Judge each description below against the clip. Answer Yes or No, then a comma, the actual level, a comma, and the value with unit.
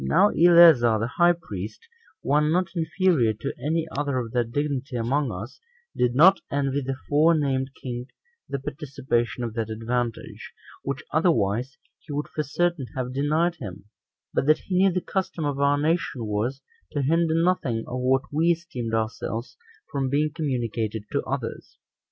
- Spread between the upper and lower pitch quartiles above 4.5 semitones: Yes, average, 5.0 semitones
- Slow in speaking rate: No, average, 160 wpm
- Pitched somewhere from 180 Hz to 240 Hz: No, medium, 140 Hz